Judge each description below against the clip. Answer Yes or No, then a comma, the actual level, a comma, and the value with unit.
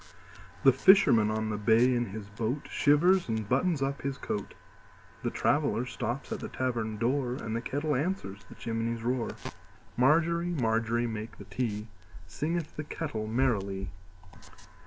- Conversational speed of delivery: No, slow, 130 wpm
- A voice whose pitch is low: Yes, low, 120 Hz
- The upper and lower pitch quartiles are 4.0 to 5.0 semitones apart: Yes, average, 4.6 semitones